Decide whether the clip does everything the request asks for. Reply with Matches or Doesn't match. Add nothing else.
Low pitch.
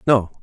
Matches